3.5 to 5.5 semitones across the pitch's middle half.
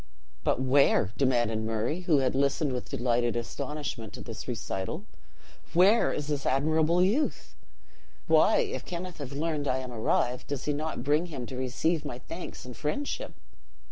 Yes: average, 4.5 semitones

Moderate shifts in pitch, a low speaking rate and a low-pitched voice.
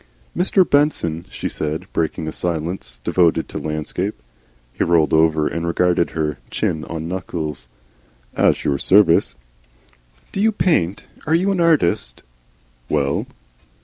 Yes: average, 4.7 semitones; slow, 130 wpm; very low, 85 Hz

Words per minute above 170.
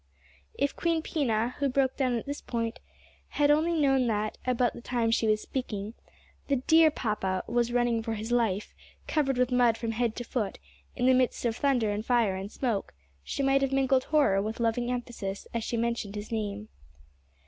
Yes: average, 190 wpm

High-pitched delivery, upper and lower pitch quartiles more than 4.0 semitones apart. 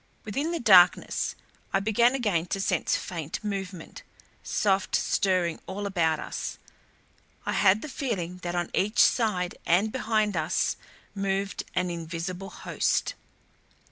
No: high, 195 Hz; average, 3.2 semitones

